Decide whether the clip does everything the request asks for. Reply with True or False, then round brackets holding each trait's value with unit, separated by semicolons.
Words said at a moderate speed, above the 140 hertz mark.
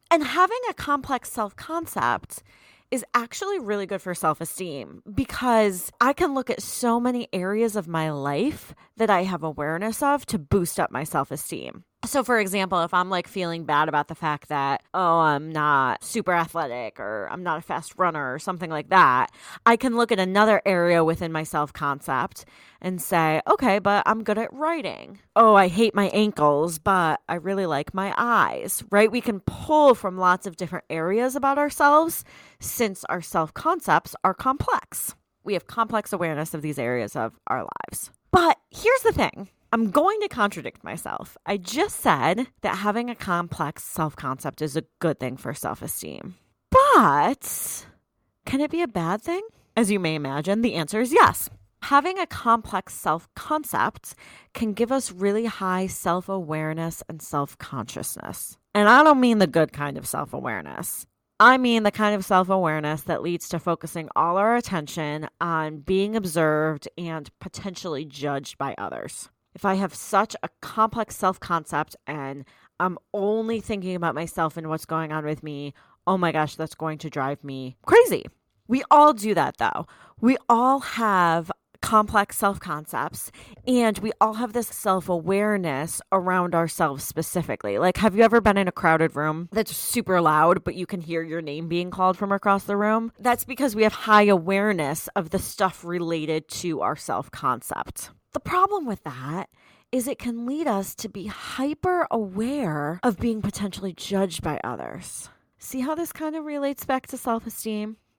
True (180 wpm; 190 Hz)